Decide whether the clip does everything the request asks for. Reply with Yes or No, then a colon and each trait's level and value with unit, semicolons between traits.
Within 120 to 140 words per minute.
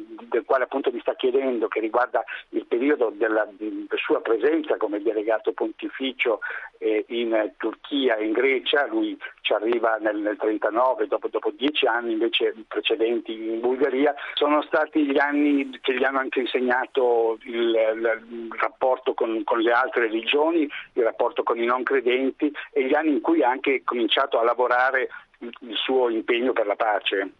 No: average, 165 wpm